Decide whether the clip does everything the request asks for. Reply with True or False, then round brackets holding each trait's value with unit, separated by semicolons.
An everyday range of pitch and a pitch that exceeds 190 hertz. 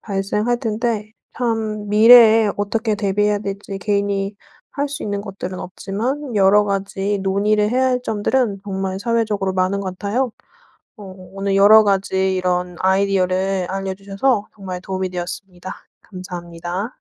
False (2.1 semitones; 200 Hz)